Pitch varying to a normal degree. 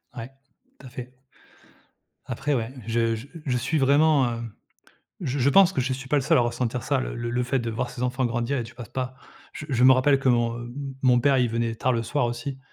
No: narrow, 2.3 semitones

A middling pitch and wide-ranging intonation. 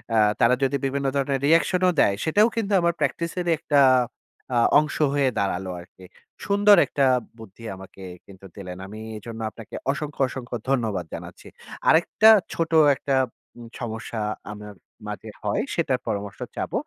No: low, 130 Hz; wide, 7.0 semitones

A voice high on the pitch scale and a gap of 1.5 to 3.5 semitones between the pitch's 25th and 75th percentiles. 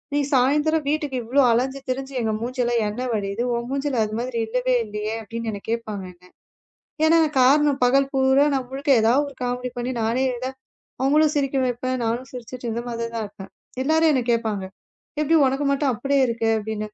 Yes: very high, 250 Hz; average, 3.2 semitones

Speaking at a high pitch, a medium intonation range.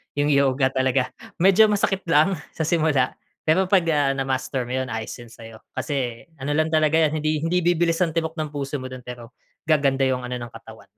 No: medium, 145 Hz; average, 3.9 semitones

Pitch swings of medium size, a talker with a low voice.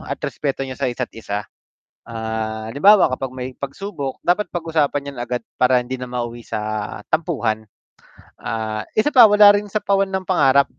No: wide, 7.0 semitones; low, 130 Hz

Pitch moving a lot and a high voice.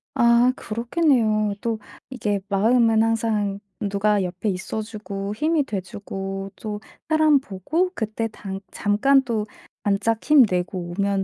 No: average, 3.0 semitones; high, 215 Hz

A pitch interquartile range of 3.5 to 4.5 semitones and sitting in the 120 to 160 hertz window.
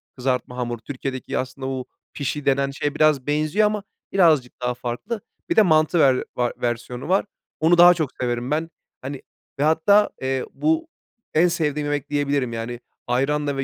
Yes: average, 3.9 semitones; medium, 140 Hz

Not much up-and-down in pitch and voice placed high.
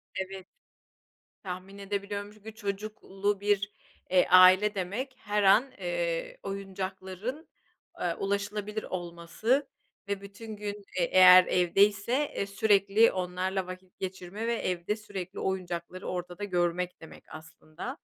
Yes: narrow, 2.3 semitones; high, 195 Hz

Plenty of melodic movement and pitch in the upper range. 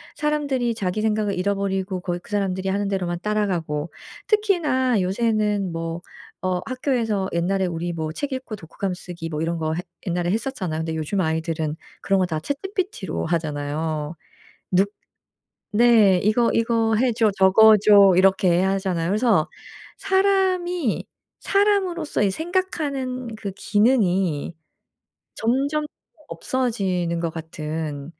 Yes: wide, 5.9 semitones; high, 195 Hz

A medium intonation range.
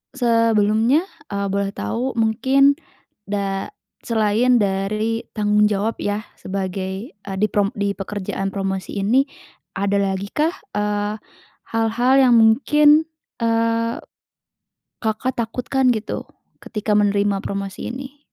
Yes: average, 3.0 semitones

